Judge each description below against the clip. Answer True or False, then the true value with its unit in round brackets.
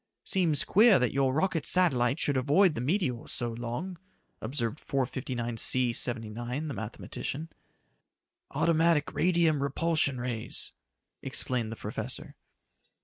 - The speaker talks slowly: True (110 wpm)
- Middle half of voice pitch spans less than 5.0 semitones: False (5.3 semitones)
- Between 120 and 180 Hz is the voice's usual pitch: True (135 Hz)